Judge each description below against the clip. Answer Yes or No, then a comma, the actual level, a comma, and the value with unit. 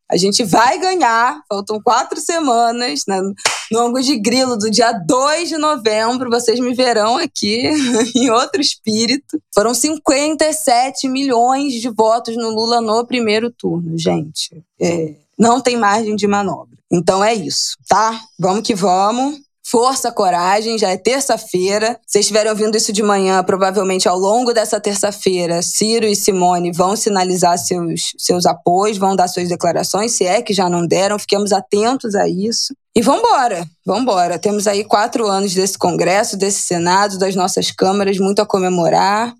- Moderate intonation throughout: Yes, average, 3.8 semitones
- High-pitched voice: Yes, high, 215 Hz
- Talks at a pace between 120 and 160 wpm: Yes, average, 155 wpm